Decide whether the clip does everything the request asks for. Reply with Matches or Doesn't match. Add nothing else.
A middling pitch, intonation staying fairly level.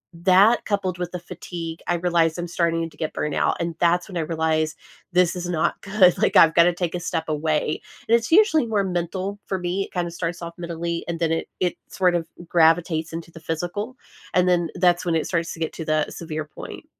Matches